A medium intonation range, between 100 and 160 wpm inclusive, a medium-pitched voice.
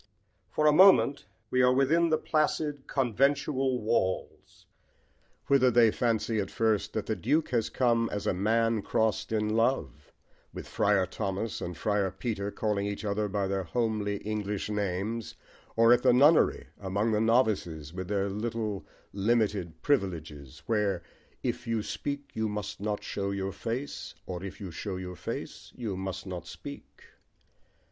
No: average, 3.7 semitones; average, 155 wpm; low, 105 Hz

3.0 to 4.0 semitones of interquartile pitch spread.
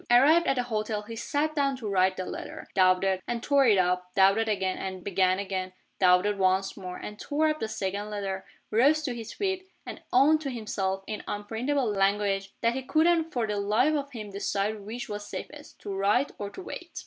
No: wide, 5.5 semitones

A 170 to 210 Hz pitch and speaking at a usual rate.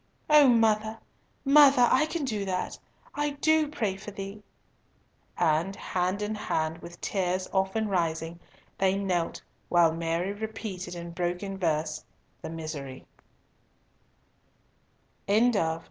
No: high, 190 Hz; slow, 115 wpm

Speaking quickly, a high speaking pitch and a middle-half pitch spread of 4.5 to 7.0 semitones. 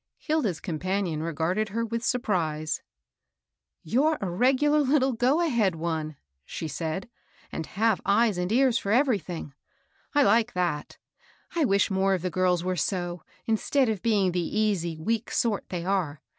No: average, 160 wpm; high, 195 Hz; average, 5.2 semitones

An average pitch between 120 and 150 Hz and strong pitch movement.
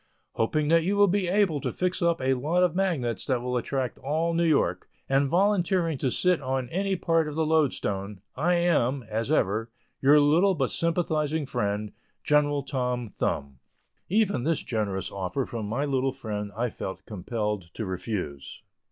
Yes: medium, 140 Hz; wide, 6.7 semitones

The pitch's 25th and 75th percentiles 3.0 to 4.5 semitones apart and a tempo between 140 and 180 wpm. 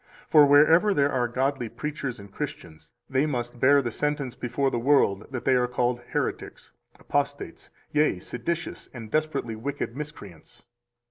Yes: average, 3.4 semitones; average, 150 wpm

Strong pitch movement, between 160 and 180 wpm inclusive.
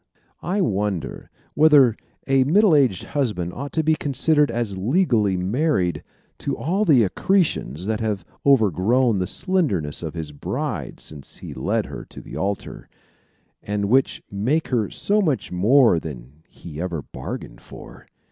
No: wide, 8.3 semitones; average, 145 wpm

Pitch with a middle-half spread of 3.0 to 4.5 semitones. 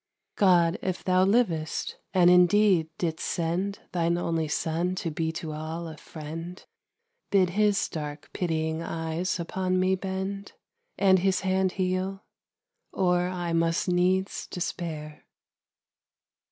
No: narrow, 2.4 semitones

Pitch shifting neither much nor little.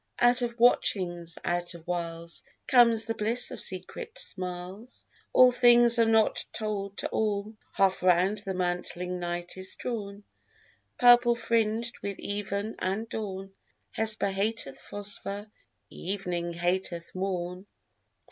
Yes: average, 3.9 semitones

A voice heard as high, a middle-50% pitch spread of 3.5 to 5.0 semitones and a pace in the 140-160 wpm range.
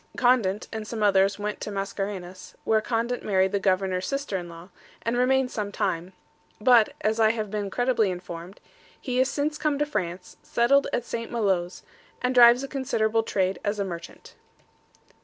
No: high, 210 Hz; average, 4.3 semitones; average, 175 wpm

